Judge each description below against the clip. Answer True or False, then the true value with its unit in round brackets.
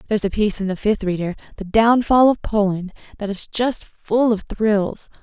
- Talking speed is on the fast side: False (185 wpm)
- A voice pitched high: True (210 Hz)